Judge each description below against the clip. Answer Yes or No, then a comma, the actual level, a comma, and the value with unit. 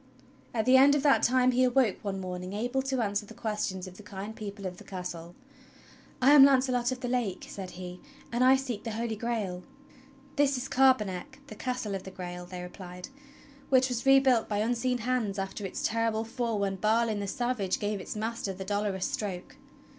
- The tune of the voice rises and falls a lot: No, average, 4.7 semitones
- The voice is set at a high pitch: Yes, high, 220 Hz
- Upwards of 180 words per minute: Yes, average, 200 wpm